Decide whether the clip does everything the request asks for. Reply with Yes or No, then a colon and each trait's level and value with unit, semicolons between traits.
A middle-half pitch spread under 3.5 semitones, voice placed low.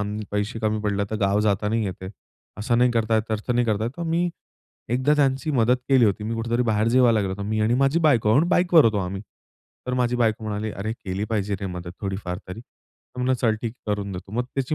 Yes: average, 3.1 semitones; low, 110 Hz